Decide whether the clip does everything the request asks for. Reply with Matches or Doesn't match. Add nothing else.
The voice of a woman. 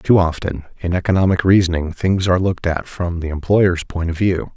Doesn't match